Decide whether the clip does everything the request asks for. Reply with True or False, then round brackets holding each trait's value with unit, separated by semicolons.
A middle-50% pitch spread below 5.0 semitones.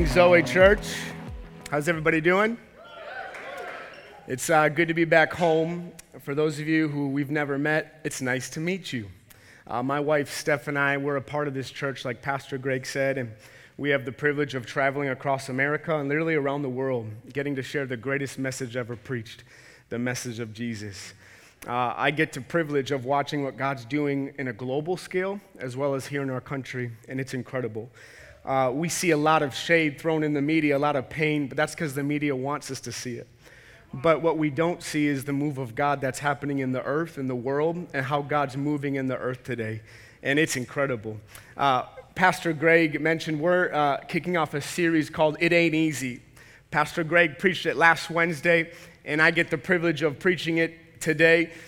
True (3.6 semitones)